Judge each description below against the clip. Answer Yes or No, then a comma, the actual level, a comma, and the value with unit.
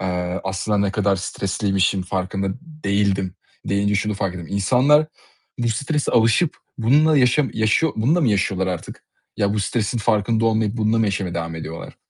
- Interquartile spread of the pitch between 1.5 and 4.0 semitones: Yes, average, 3.4 semitones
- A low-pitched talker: Yes, low, 105 Hz